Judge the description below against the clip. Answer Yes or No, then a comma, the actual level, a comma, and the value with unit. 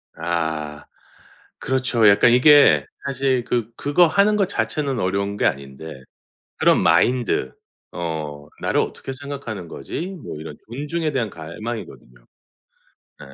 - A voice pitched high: No, low, 115 Hz